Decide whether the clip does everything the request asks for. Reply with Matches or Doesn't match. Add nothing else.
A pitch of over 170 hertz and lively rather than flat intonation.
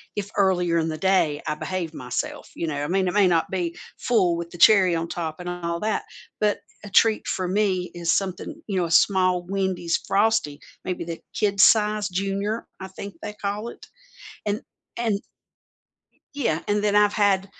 Doesn't match